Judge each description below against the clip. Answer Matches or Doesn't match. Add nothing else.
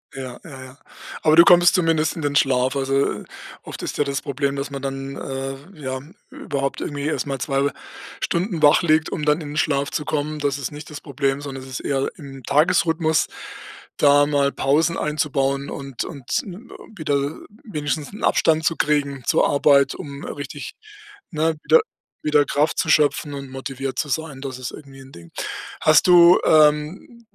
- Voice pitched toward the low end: Doesn't match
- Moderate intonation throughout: Doesn't match